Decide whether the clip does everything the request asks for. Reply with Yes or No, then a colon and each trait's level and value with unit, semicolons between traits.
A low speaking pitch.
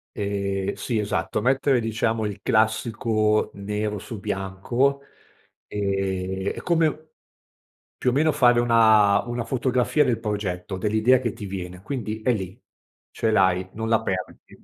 Yes: low, 110 Hz